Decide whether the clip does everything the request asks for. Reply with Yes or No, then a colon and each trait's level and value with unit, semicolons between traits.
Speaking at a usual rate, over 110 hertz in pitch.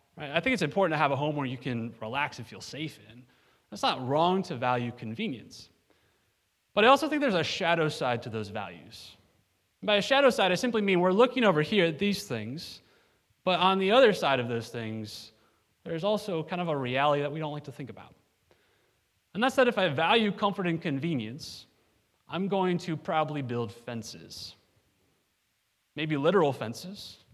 Yes: average, 195 wpm; medium, 140 Hz